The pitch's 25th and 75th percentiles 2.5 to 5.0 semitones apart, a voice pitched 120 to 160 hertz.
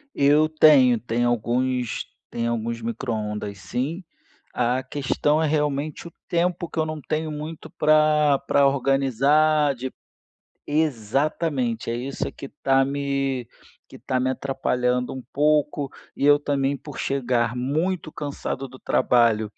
Yes: average, 3.4 semitones; low, 135 Hz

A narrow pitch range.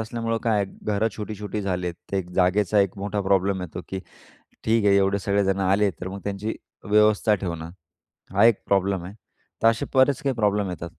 Yes: narrow, 1.9 semitones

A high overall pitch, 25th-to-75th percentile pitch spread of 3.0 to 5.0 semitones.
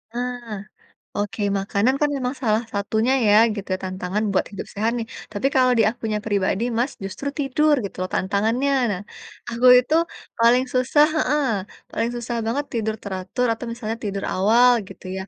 Yes: high, 225 Hz; average, 3.7 semitones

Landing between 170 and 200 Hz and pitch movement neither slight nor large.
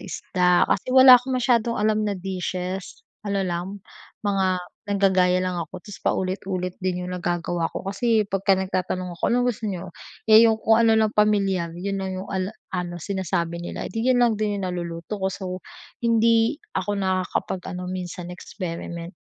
Yes: high, 190 Hz; average, 3.0 semitones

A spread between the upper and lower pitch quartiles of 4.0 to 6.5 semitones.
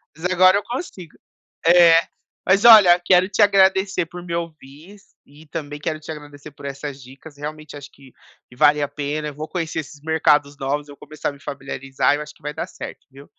No: average, 3.6 semitones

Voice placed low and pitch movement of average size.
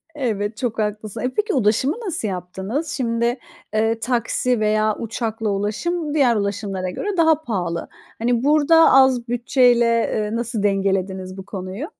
No: high, 230 Hz; average, 4.0 semitones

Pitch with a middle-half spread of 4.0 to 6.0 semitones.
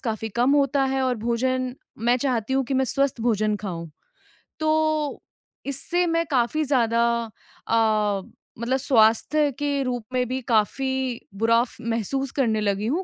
No: average, 3.4 semitones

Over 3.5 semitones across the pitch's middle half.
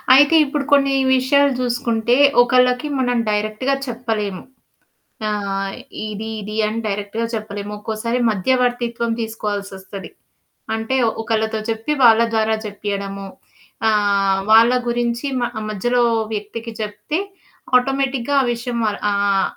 No: average, 3.1 semitones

